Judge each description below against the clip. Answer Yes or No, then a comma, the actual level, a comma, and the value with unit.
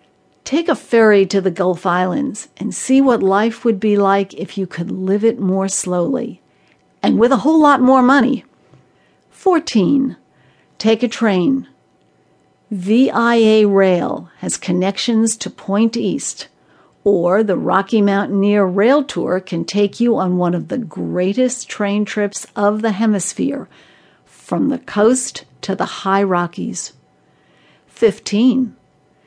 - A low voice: No, high, 210 Hz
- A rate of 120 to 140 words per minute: Yes, slow, 135 wpm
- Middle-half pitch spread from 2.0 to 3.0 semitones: No, average, 3.5 semitones